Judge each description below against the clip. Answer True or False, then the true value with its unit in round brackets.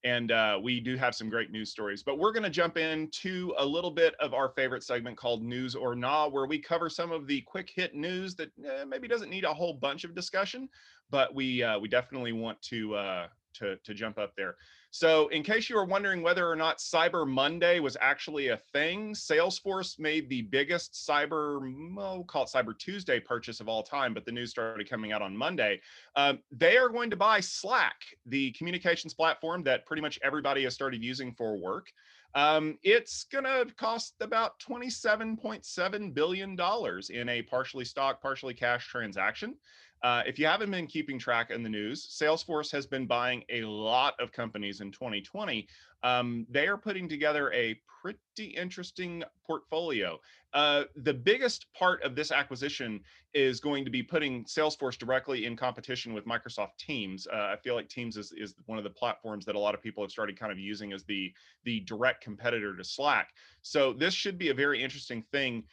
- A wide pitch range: True (6.6 semitones)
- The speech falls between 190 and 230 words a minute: True (195 wpm)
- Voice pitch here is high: False (140 Hz)